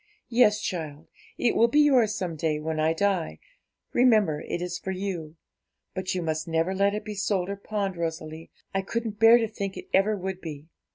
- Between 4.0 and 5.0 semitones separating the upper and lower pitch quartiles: Yes, average, 4.5 semitones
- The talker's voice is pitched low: No, high, 190 Hz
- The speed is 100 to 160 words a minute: No, average, 195 wpm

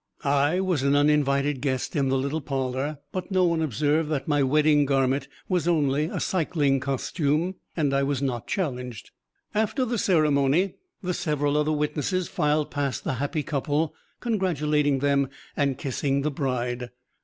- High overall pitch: No, medium, 145 Hz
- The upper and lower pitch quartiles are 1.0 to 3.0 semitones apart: Yes, narrow, 2.4 semitones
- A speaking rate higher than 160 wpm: No, average, 155 wpm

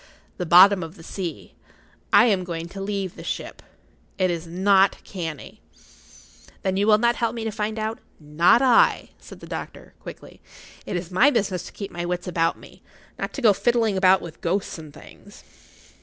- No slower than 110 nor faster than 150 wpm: No, average, 185 wpm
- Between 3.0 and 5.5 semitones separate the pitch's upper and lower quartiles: Yes, average, 3.6 semitones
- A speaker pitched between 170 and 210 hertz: Yes, high, 190 Hz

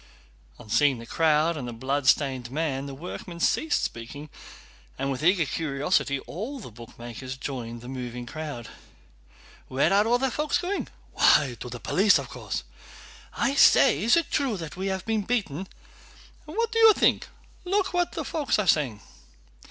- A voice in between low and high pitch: Yes, medium, 150 Hz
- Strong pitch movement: Yes, wide, 8.4 semitones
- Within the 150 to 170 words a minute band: Yes, average, 165 wpm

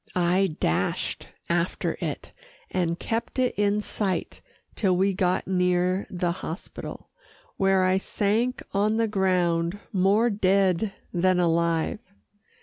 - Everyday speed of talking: No, slow, 120 wpm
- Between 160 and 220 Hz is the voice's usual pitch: Yes, medium, 185 Hz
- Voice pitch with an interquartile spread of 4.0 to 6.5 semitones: No, narrow, 2.4 semitones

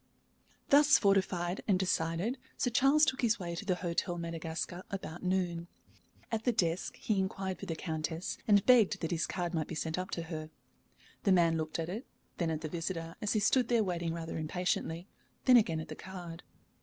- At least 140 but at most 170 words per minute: No, average, 195 wpm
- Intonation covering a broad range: No, average, 3.6 semitones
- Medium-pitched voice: Yes, medium, 180 Hz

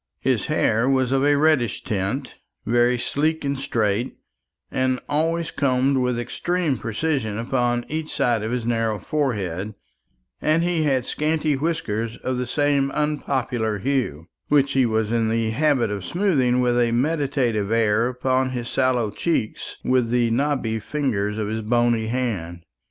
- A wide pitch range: No, average, 3.9 semitones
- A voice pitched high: No, low, 125 Hz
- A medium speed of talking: Yes, average, 150 wpm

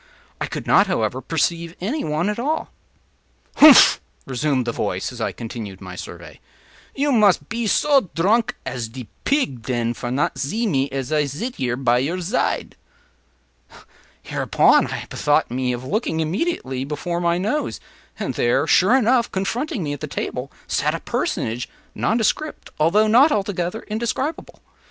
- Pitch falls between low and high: Yes, medium, 170 Hz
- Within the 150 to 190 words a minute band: Yes, average, 155 wpm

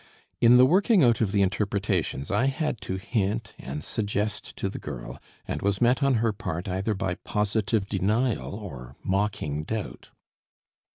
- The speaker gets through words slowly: No, average, 160 wpm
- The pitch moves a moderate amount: Yes, average, 3.3 semitones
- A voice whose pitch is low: Yes, low, 105 Hz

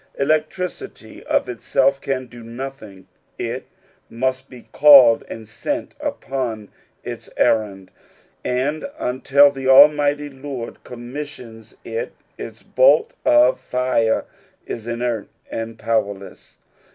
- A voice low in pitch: Yes, low, 130 Hz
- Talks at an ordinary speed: No, slow, 110 wpm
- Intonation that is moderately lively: Yes, average, 4.0 semitones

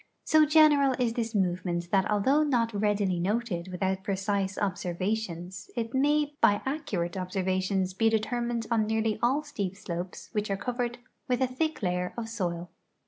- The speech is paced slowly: No, average, 160 wpm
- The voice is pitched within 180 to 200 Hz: No, high, 210 Hz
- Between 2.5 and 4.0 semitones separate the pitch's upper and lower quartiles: No, average, 4.4 semitones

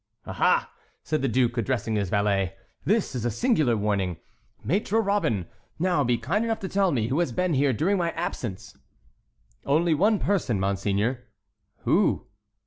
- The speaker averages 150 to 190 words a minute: Yes, average, 155 wpm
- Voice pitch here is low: Yes, low, 130 Hz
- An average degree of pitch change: No, wide, 9.0 semitones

